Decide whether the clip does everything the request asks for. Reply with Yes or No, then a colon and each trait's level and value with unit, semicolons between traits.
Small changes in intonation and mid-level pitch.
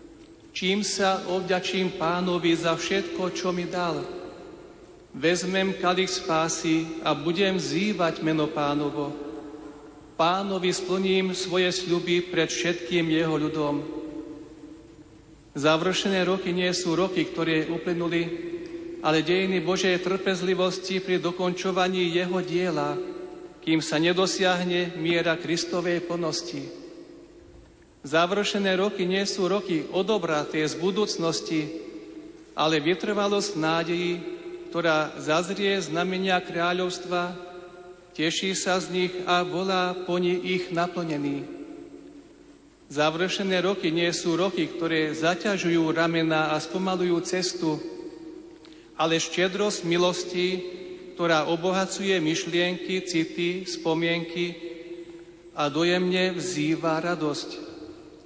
Yes: narrow, 2.3 semitones; medium, 180 Hz